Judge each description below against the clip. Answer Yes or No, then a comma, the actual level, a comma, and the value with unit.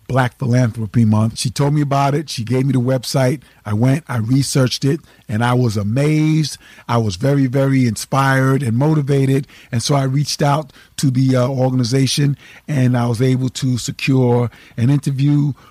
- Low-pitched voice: Yes, low, 130 Hz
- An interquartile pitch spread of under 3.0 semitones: Yes, narrow, 2.4 semitones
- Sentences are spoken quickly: No, average, 175 wpm